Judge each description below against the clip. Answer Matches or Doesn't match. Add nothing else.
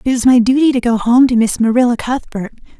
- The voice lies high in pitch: Matches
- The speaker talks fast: Matches